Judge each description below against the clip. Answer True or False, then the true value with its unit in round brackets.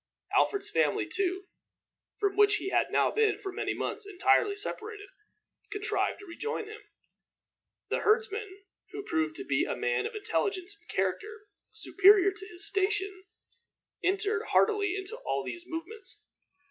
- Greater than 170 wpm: False (145 wpm)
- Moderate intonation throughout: False (1.9 semitones)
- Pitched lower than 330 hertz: False (410 Hz)